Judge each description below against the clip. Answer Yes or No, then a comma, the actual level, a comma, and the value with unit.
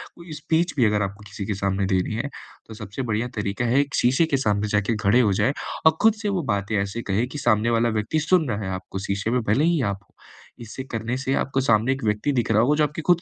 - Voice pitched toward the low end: Yes, low, 115 Hz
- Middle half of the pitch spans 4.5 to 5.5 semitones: Yes, average, 4.9 semitones